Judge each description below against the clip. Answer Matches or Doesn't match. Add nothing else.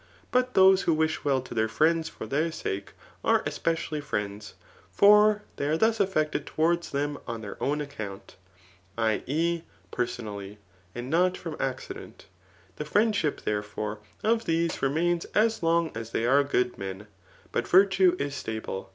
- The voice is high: Doesn't match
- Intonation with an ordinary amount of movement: Doesn't match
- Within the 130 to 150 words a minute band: Doesn't match